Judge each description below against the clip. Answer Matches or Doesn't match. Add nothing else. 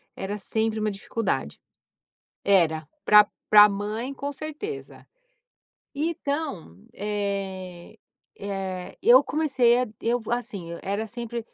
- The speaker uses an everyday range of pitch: Matches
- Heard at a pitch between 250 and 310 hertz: Doesn't match